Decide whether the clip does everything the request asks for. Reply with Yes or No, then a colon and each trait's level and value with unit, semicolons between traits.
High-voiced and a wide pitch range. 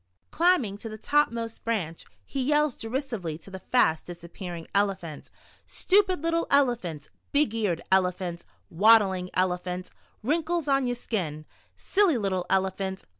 Yes: high, 205 Hz; wide, 7.3 semitones